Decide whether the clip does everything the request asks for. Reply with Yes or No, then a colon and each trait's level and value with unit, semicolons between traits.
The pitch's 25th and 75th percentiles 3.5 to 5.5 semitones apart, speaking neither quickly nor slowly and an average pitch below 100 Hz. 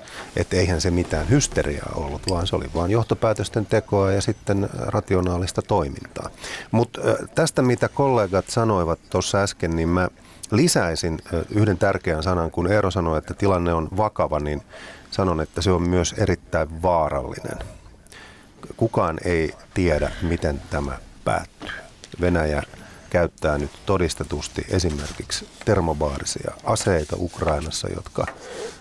Yes: average, 4.0 semitones; average, 125 wpm; very low, 90 Hz